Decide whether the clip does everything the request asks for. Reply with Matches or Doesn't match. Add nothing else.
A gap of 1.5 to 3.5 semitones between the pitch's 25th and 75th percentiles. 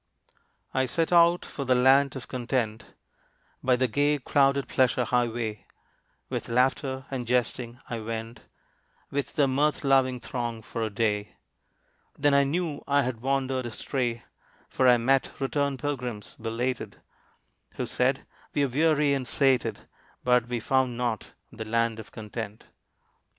Matches